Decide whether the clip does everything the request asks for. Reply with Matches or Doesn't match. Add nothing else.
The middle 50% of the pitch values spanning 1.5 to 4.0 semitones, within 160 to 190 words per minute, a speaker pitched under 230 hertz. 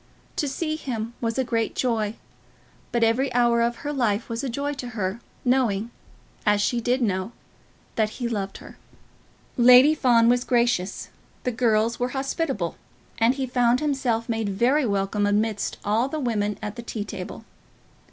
Doesn't match